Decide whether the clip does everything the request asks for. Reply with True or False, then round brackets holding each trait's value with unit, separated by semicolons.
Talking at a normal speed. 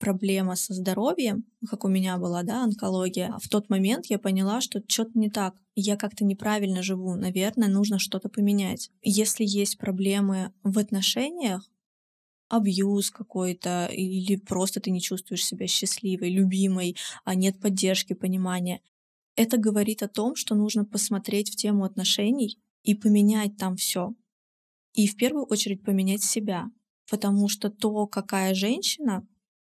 True (140 wpm)